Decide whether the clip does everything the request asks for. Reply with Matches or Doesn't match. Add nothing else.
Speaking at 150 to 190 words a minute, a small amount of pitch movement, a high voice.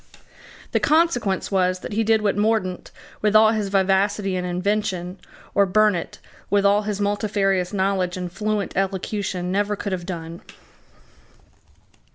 Doesn't match